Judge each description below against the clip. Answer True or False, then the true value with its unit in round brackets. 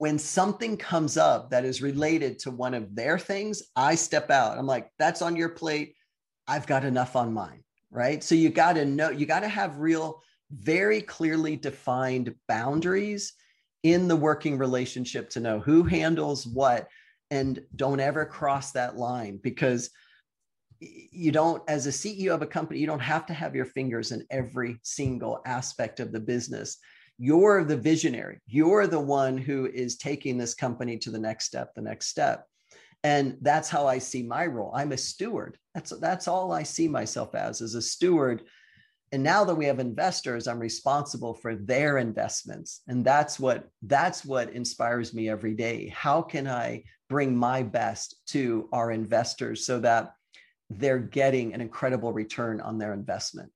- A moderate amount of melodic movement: True (4.5 semitones)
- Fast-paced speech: False (175 wpm)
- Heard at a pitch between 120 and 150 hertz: True (135 Hz)